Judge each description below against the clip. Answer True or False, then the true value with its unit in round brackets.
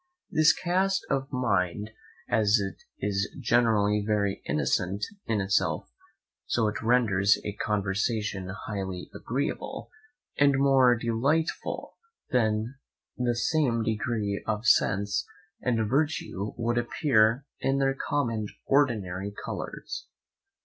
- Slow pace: True (110 wpm)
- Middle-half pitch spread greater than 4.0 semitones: True (4.4 semitones)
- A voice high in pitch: False (115 Hz)